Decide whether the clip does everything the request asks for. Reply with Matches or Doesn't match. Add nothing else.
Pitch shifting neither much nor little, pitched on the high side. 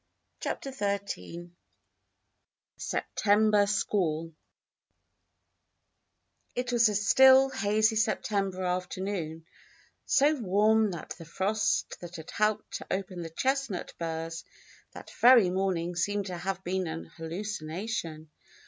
Matches